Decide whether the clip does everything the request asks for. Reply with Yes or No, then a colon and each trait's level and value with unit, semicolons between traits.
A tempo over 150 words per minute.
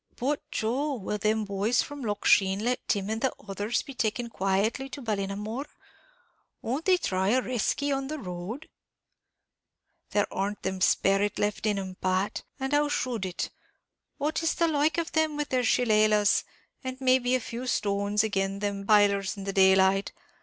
Yes: average, 175 wpm